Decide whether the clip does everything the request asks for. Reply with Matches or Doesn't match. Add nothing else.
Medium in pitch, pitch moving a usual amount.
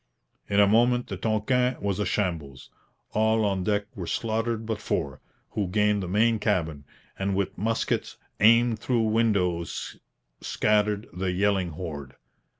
Doesn't match